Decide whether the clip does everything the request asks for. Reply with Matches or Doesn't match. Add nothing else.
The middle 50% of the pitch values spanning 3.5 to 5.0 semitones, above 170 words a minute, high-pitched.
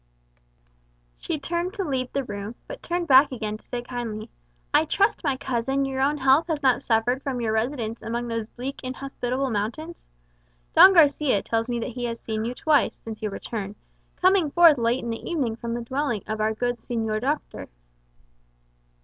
Matches